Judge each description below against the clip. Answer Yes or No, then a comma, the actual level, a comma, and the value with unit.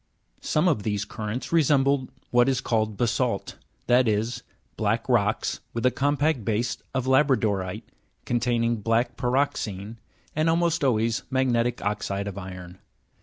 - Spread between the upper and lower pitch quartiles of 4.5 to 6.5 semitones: No, average, 3.8 semitones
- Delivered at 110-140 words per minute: Yes, slow, 135 wpm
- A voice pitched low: Yes, low, 120 Hz